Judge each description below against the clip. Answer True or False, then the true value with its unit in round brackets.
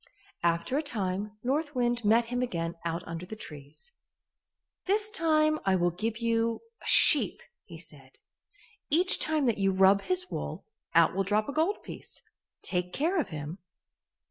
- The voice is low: False (225 Hz)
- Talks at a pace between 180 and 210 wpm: False (165 wpm)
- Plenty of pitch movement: True (8.8 semitones)